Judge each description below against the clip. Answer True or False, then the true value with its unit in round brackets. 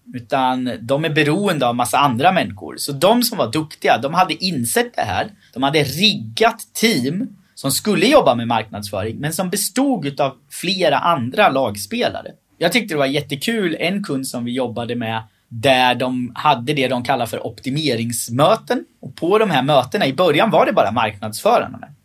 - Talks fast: False (175 wpm)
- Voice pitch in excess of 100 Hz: True (140 Hz)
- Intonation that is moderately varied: False (7.2 semitones)